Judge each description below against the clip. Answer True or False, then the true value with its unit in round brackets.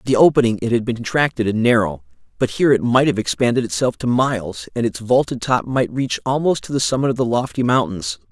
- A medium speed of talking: False (230 wpm)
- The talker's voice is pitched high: False (120 Hz)